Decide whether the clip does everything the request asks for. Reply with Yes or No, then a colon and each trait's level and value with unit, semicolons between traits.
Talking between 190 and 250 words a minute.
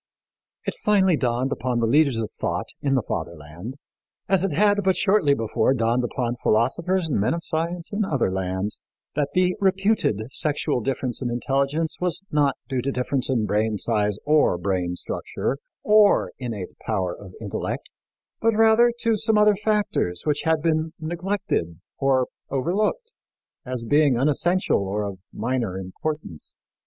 No: average, 155 wpm